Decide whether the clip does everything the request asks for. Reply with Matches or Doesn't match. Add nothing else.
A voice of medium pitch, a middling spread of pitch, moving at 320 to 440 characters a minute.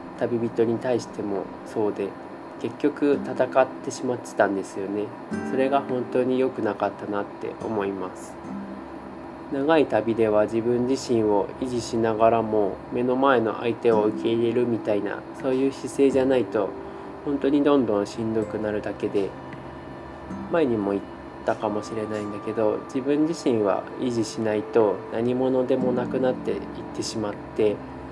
Doesn't match